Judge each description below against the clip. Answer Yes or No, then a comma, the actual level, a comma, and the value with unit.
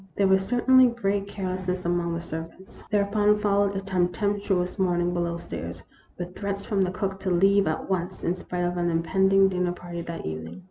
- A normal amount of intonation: No, narrow, 2.3 semitones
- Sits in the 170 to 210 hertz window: Yes, medium, 185 Hz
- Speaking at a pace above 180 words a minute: Yes, average, 190 wpm